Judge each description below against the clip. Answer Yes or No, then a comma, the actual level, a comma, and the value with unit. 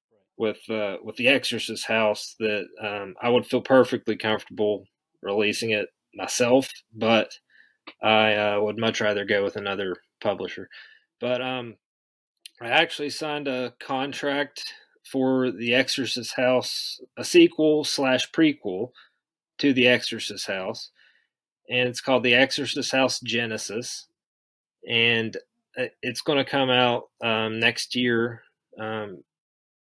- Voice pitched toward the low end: Yes, low, 125 Hz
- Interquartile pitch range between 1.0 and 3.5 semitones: Yes, average, 3.0 semitones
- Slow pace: Yes, slow, 125 wpm